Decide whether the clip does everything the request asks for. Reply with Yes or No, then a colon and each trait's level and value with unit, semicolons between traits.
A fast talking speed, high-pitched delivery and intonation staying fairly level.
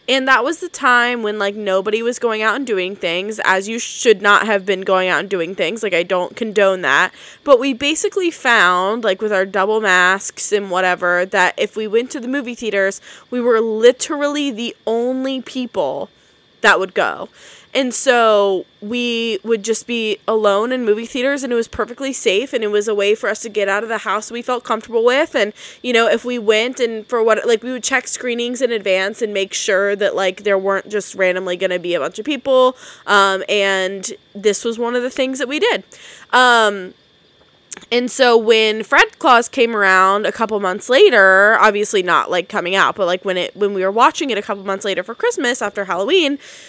No: fast, 215 wpm; high, 220 Hz; average, 3.8 semitones